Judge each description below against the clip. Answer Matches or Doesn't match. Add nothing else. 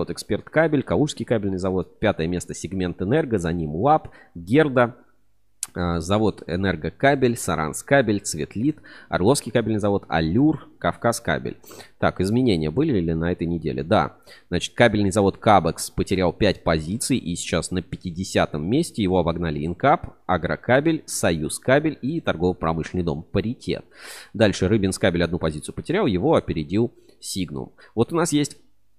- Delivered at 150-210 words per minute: Doesn't match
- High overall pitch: Doesn't match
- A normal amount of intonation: Doesn't match